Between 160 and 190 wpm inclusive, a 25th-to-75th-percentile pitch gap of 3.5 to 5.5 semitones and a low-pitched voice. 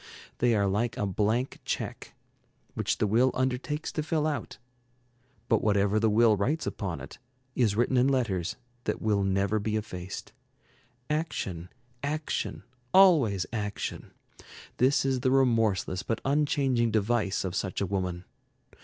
No: average, 140 wpm; average, 4.6 semitones; low, 110 Hz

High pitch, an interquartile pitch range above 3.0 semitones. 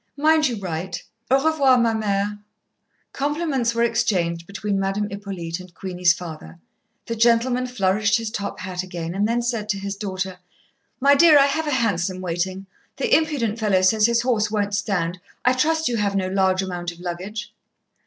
Yes: high, 205 Hz; average, 4.4 semitones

